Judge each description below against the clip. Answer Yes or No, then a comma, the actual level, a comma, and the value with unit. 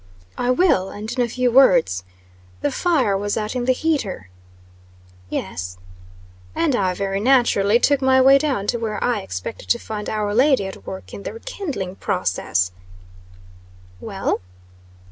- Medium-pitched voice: No, high, 215 Hz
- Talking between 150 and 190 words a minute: Yes, average, 155 wpm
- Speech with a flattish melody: No, wide, 5.4 semitones